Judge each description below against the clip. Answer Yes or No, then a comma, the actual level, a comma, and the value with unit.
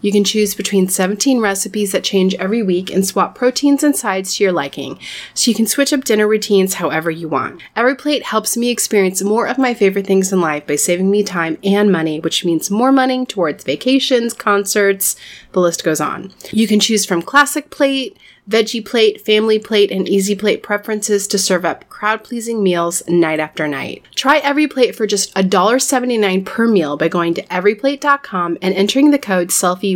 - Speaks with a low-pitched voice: No, high, 205 Hz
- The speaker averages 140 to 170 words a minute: No, average, 190 wpm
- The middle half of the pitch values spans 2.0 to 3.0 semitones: No, average, 3.9 semitones